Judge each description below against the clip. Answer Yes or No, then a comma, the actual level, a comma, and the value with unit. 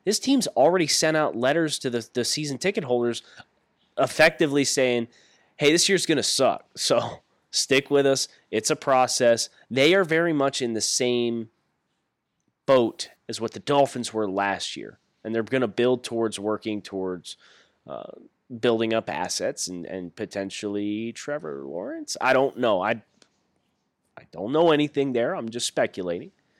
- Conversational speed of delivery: Yes, average, 160 wpm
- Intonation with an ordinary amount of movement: Yes, average, 5.0 semitones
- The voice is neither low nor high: No, low, 120 Hz